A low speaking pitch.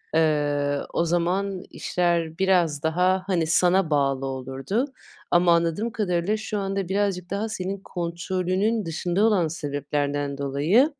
No: medium, 175 Hz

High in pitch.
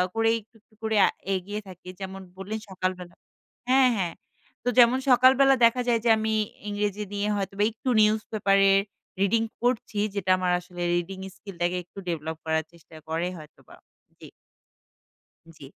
Yes: high, 200 Hz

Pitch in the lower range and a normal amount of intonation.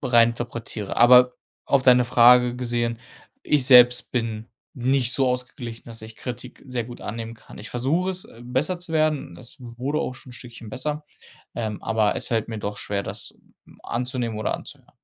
No: low, 120 Hz; narrow, 1.9 semitones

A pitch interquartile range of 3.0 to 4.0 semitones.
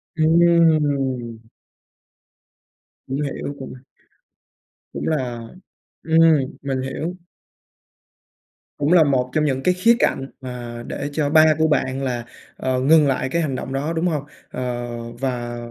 Yes: average, 3.7 semitones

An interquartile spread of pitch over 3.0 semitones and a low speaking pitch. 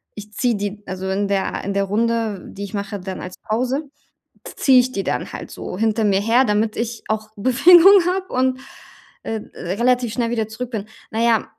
No: average, 3.5 semitones; high, 220 Hz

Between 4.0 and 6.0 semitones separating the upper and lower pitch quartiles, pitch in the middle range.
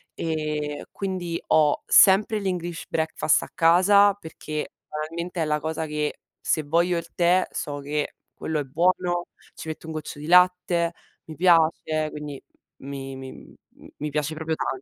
No: narrow, 2.6 semitones; medium, 160 Hz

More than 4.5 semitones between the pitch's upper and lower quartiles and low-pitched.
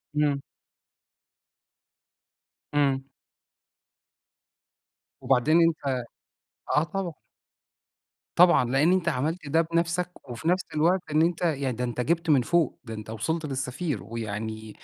No: average, 5.1 semitones; medium, 145 Hz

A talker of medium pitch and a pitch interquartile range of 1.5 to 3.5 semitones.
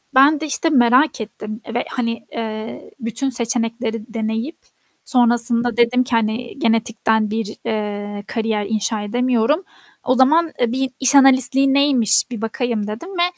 No: high, 235 Hz; average, 2.8 semitones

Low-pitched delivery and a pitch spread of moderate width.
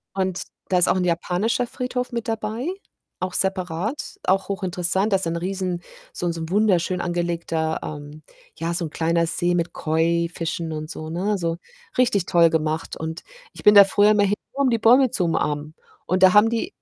No: medium, 180 Hz; average, 3.6 semitones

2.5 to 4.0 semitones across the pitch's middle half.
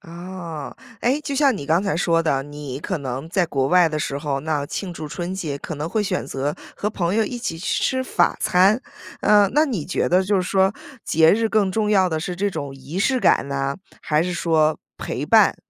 No: average, 4.9 semitones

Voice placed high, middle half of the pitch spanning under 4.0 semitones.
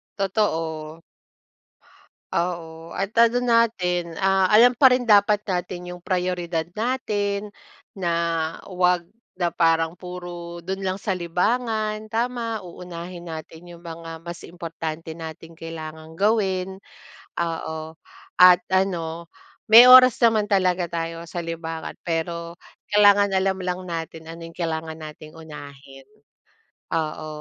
No: medium, 175 Hz; average, 3.2 semitones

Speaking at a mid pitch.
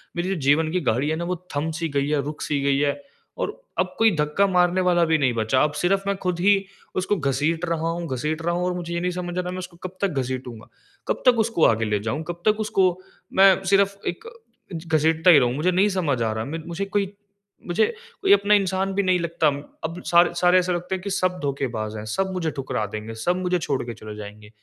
Yes: medium, 170 Hz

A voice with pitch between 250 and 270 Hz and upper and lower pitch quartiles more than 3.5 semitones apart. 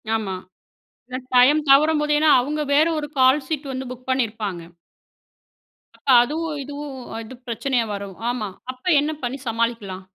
Yes: very high, 260 Hz; average, 4.4 semitones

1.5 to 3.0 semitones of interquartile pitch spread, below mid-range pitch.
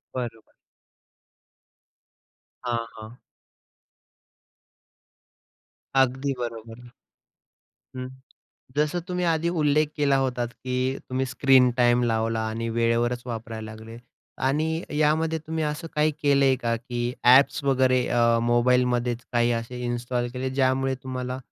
Yes: average, 2.7 semitones; low, 125 Hz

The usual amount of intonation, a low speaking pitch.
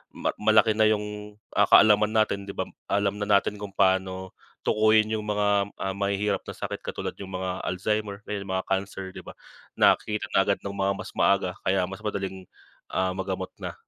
No: narrow, 1.6 semitones; low, 100 Hz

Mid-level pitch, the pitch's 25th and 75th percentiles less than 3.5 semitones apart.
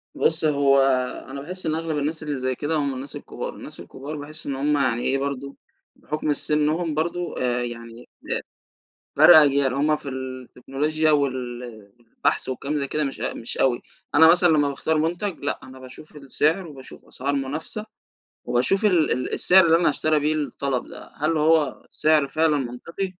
Yes: medium, 145 Hz; average, 2.8 semitones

